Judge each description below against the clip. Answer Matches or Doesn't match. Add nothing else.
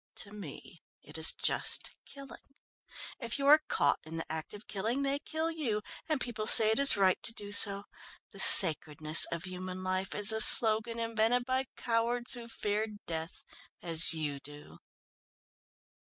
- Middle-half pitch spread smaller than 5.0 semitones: Doesn't match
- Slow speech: Doesn't match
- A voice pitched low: Doesn't match